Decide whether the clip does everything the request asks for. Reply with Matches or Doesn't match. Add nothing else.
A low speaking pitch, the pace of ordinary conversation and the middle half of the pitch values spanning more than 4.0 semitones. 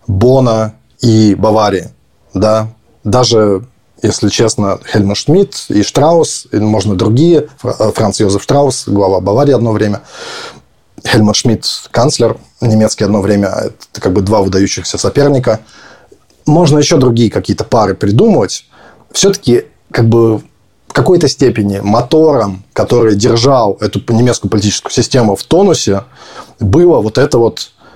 Doesn't match